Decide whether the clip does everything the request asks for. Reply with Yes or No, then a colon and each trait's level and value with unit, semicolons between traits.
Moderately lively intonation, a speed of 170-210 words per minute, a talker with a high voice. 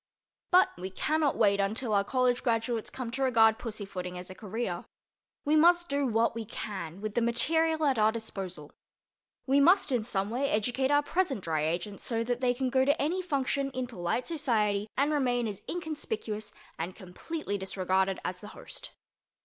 No: wide, 5.7 semitones; average, 180 wpm; high, 230 Hz